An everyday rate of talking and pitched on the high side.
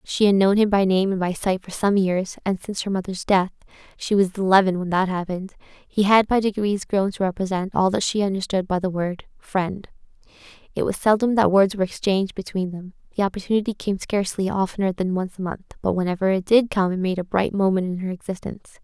No: fast, 220 wpm; high, 195 Hz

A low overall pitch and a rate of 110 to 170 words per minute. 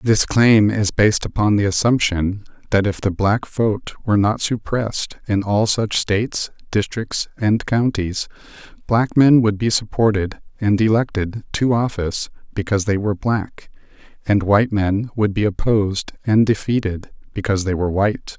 Yes: low, 105 Hz; average, 155 wpm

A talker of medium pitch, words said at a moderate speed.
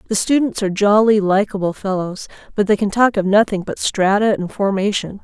No: high, 205 Hz; average, 185 wpm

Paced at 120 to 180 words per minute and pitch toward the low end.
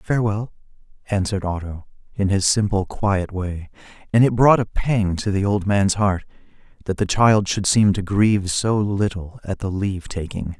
Yes: average, 175 wpm; low, 100 Hz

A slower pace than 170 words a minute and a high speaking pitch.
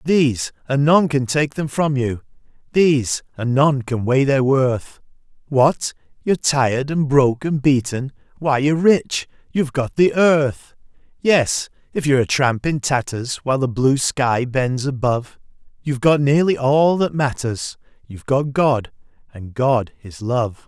No: average, 155 wpm; low, 135 Hz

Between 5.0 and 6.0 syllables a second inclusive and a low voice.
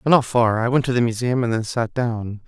Yes: 5.6 syllables/s; low, 120 Hz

